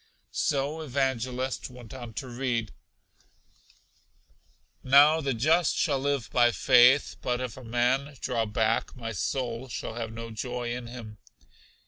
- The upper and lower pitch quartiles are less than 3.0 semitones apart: Yes, narrow, 2.6 semitones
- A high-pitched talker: No, low, 125 Hz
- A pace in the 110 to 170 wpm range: Yes, slow, 135 wpm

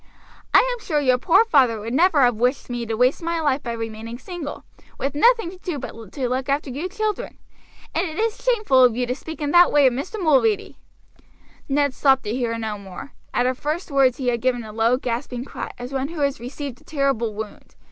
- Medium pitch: No, very high, 265 Hz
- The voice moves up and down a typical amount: Yes, average, 4.4 semitones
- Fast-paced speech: Yes, fast, 225 wpm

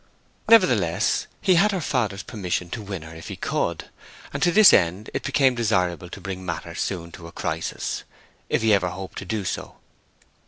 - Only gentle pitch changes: No, average, 5.1 semitones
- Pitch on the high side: No, very low, 95 Hz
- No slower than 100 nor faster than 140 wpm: No, average, 190 wpm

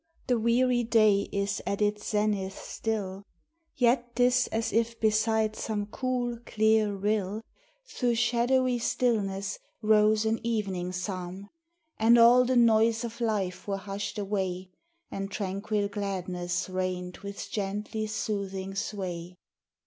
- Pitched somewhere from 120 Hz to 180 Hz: No, high, 210 Hz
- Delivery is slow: Yes, slow, 125 wpm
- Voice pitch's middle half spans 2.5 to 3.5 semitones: Yes, average, 2.8 semitones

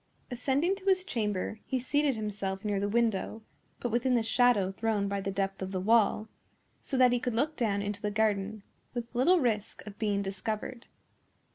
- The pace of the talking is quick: No, average, 185 wpm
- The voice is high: Yes, high, 220 Hz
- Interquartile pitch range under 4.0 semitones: Yes, average, 3.5 semitones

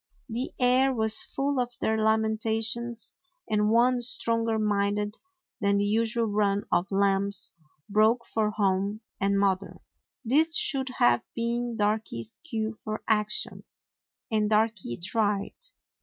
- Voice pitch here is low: No, high, 220 Hz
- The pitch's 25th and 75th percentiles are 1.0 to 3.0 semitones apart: Yes, narrow, 2.4 semitones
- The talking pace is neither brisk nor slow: No, slow, 125 wpm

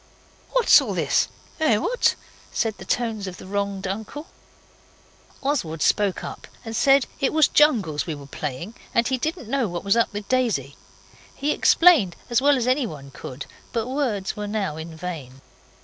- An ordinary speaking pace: Yes, average, 170 wpm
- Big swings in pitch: Yes, wide, 6.9 semitones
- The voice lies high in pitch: Yes, high, 215 Hz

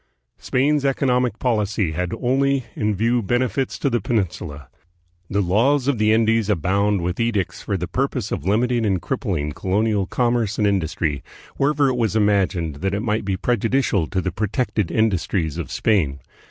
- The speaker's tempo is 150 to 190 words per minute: Yes, average, 165 wpm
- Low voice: Yes, low, 105 Hz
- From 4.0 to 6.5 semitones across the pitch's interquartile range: Yes, average, 4.6 semitones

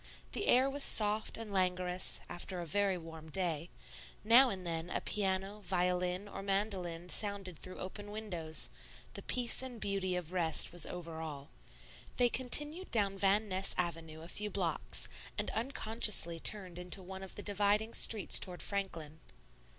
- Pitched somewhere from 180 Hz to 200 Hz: Yes, high, 190 Hz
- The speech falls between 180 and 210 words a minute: No, average, 160 wpm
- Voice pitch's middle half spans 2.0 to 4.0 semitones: Yes, average, 3.1 semitones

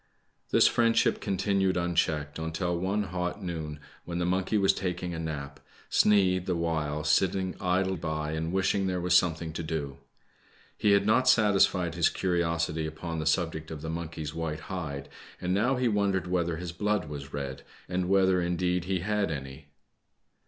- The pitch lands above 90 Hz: No, very low, 85 Hz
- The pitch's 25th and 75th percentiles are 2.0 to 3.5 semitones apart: Yes, average, 3.1 semitones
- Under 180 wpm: Yes, average, 170 wpm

